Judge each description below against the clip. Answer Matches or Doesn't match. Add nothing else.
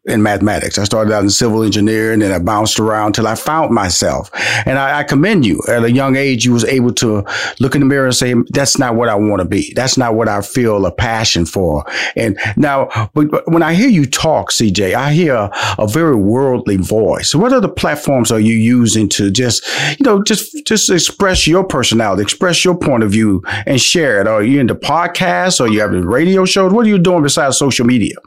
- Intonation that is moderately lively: Doesn't match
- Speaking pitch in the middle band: Doesn't match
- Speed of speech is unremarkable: Doesn't match